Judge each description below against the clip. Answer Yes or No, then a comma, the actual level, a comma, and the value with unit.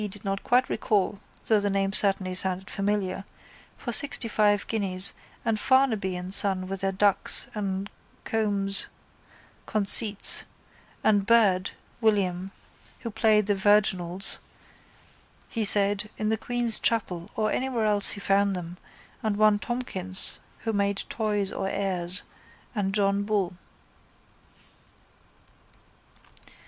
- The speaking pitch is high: Yes, high, 200 Hz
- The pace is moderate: No, slow, 120 wpm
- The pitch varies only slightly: Yes, narrow, 1.9 semitones